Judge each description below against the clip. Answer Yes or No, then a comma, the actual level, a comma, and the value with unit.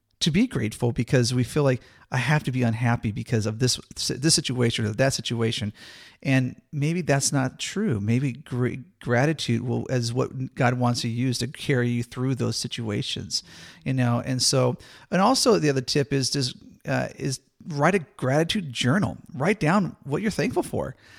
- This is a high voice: No, low, 130 Hz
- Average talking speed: Yes, average, 180 wpm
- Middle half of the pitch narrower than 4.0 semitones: Yes, average, 3.4 semitones